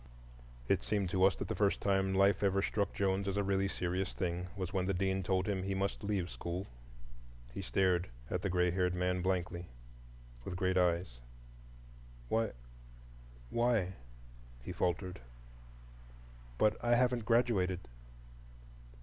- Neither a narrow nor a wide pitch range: No, narrow, 1.9 semitones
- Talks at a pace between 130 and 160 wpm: Yes, average, 140 wpm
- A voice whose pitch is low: Yes, very low, 95 Hz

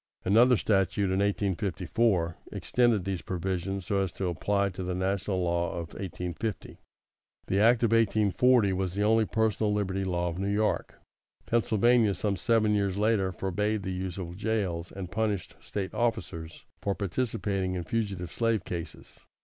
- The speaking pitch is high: No, low, 100 Hz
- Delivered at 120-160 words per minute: Yes, average, 155 wpm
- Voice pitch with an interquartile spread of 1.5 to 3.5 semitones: Yes, average, 2.9 semitones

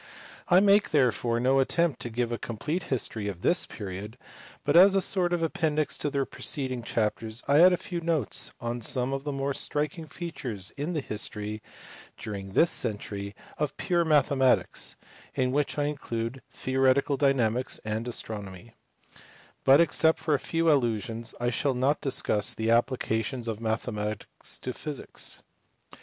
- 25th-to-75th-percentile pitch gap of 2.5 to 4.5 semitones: No, average, 5.0 semitones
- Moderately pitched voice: No, low, 130 Hz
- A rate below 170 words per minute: Yes, average, 160 wpm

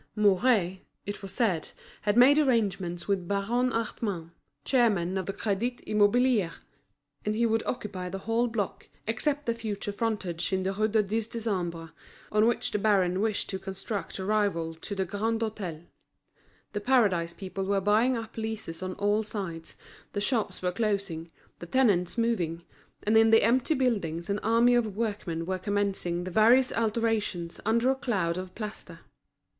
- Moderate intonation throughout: Yes, average, 3.4 semitones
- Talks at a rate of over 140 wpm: Yes, average, 165 wpm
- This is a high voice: Yes, high, 205 Hz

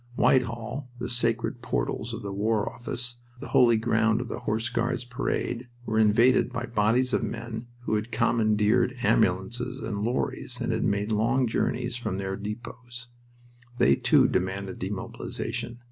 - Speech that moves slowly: No, average, 150 wpm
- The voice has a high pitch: No, low, 115 Hz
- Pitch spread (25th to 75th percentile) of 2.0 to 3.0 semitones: Yes, narrow, 2.4 semitones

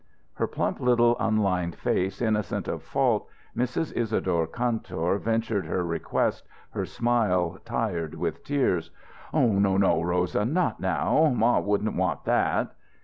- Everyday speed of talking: No, slow, 130 wpm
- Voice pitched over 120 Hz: No, low, 100 Hz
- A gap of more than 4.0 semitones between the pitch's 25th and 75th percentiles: Yes, average, 4.7 semitones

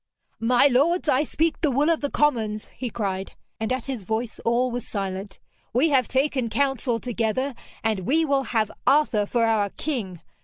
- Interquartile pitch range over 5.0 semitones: No, average, 4.2 semitones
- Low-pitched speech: No, high, 245 Hz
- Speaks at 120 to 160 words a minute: No, average, 180 wpm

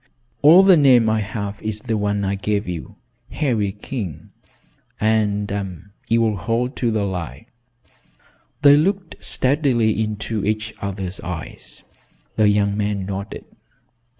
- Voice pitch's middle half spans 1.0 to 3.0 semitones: Yes, narrow, 2.6 semitones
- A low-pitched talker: Yes, low, 105 Hz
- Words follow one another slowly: Yes, slow, 130 wpm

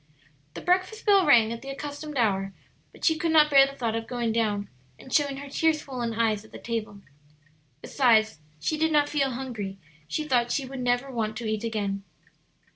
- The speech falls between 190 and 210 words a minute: Yes, average, 200 wpm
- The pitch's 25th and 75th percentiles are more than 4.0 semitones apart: Yes, average, 4.7 semitones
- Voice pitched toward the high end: Yes, high, 245 Hz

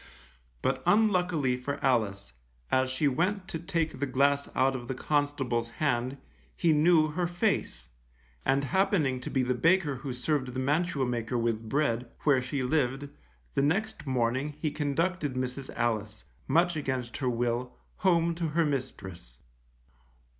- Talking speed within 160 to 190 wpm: No, average, 150 wpm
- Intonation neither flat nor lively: Yes, average, 4.3 semitones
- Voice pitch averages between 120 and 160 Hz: Yes, low, 135 Hz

